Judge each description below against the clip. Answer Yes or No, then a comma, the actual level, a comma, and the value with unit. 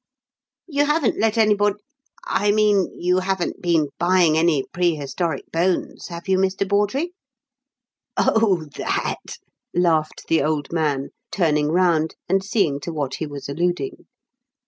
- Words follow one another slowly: Yes, slow, 130 wpm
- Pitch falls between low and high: Yes, medium, 175 Hz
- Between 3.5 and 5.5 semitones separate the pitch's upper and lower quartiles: Yes, average, 4.3 semitones